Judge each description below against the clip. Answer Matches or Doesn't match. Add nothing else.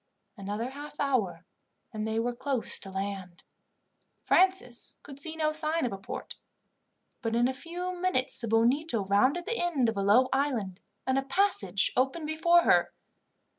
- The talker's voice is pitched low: Doesn't match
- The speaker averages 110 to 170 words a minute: Matches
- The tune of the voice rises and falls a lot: Matches